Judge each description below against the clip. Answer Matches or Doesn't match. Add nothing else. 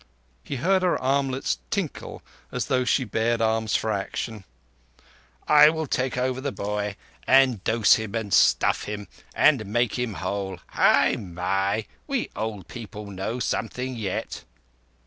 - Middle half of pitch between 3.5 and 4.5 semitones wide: Matches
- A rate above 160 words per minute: Doesn't match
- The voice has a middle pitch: Doesn't match